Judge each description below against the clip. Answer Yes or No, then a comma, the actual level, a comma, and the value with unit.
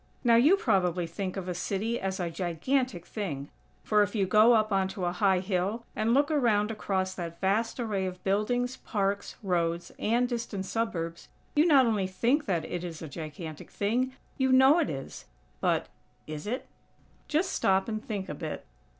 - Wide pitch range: No, average, 4.6 semitones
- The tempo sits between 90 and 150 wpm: No, average, 180 wpm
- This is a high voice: Yes, high, 200 Hz